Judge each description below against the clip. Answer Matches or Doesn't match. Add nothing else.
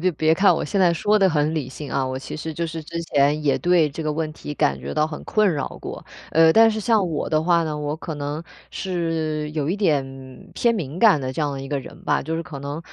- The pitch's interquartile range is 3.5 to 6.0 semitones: Doesn't match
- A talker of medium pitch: Matches